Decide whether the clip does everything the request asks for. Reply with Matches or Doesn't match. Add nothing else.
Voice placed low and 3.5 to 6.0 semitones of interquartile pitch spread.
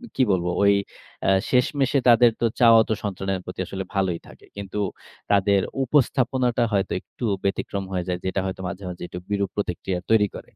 Matches